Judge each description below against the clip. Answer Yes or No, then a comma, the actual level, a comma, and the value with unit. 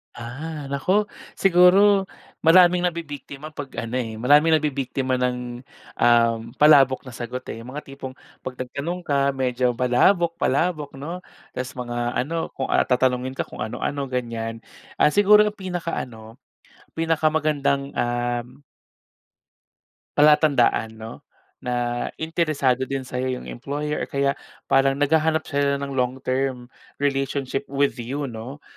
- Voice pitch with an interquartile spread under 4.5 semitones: Yes, average, 3.6 semitones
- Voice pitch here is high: No, low, 135 Hz